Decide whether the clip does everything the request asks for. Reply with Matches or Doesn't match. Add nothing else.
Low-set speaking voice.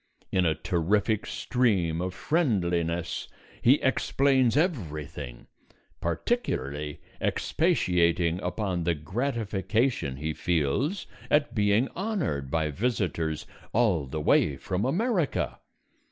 Matches